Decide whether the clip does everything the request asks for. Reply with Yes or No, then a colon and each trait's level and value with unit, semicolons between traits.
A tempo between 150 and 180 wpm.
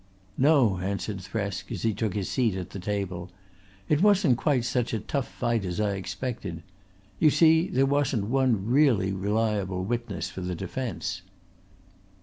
Yes: average, 155 wpm